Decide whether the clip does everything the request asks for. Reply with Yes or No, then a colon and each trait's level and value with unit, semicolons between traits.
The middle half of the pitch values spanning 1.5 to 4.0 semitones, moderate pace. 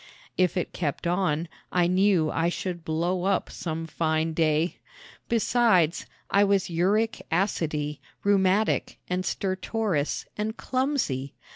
No: average, 3.7 semitones; slow, 120 wpm